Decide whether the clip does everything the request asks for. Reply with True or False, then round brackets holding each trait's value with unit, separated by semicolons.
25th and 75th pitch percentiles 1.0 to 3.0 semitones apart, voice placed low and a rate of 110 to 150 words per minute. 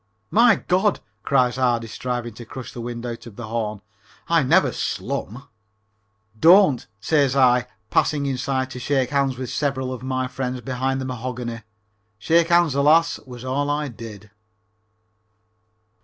True (2.7 semitones; 130 Hz; 145 wpm)